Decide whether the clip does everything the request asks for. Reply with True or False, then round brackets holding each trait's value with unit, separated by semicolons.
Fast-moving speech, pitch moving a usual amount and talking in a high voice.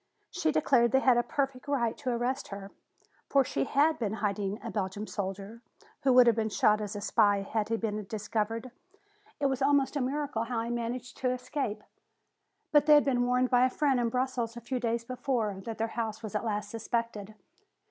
True (210 wpm; 3.2 semitones; 235 Hz)